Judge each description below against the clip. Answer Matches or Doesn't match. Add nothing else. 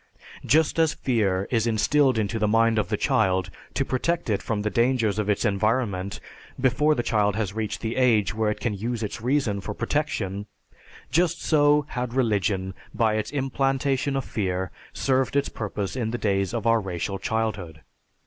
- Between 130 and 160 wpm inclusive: Doesn't match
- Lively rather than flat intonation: Doesn't match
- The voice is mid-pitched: Doesn't match